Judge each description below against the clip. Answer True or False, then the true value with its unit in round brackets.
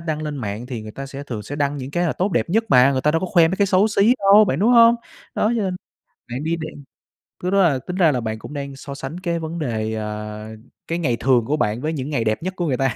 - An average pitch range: False (5.9 semitones)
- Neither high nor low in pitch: True (145 Hz)